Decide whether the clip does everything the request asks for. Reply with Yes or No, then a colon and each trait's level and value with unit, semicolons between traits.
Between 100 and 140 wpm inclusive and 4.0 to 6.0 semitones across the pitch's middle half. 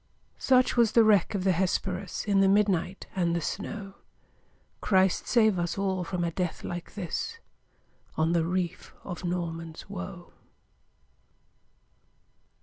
No: slow, 135 wpm; narrow, 2.6 semitones